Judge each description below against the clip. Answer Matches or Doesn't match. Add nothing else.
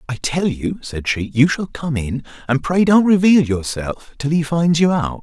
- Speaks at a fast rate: Matches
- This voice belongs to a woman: Doesn't match